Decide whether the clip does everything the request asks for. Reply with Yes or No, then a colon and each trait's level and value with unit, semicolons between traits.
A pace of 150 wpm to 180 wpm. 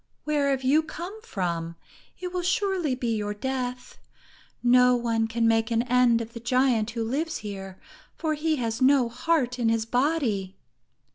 Yes: average, 165 wpm